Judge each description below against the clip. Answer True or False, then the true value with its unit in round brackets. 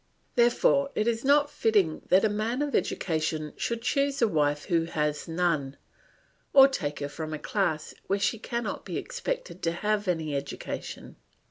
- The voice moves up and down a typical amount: False (7.3 semitones)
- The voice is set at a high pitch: True (195 Hz)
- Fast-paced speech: False (165 wpm)